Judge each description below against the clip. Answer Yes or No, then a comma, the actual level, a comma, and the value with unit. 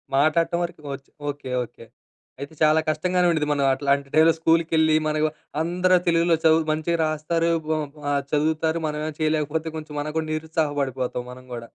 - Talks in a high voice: No, medium, 155 Hz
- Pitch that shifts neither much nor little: No, narrow, 1.9 semitones